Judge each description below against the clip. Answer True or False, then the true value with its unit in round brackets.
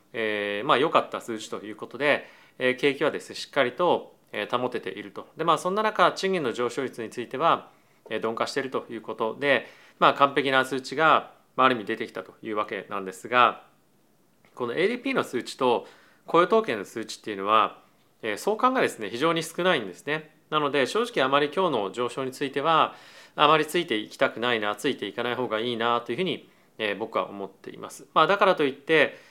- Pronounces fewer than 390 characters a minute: False (415 characters per minute)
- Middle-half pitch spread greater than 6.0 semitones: False (5.4 semitones)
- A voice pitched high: False (140 Hz)